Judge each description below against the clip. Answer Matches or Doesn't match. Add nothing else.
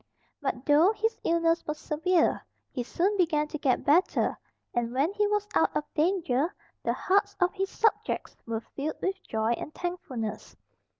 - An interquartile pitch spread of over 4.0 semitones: Matches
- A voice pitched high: Matches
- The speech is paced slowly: Doesn't match